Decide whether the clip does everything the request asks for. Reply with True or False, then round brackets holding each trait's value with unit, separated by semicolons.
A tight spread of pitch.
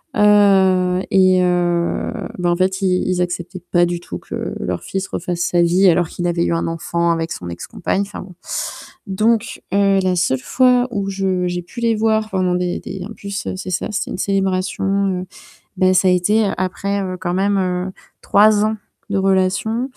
True (2.0 semitones)